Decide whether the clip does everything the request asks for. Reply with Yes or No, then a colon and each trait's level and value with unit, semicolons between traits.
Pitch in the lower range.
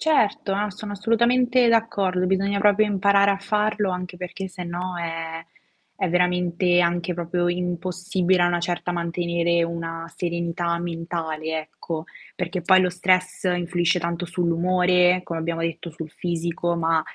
No: medium, 180 Hz